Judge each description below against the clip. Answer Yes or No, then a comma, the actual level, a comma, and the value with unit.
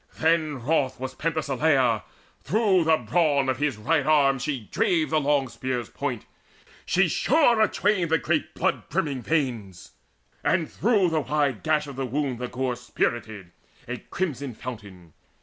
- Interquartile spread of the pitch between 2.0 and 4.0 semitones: No, average, 4.5 semitones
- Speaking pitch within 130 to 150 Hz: Yes, medium, 140 Hz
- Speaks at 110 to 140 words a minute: No, average, 150 wpm